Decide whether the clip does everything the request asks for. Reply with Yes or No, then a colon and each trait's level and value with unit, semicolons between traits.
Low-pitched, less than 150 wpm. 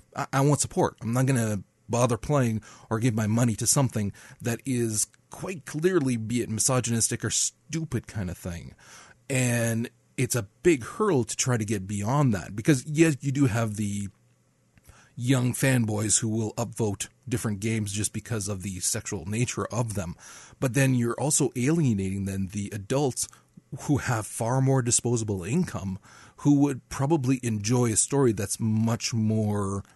No: low, 120 Hz; average, 165 wpm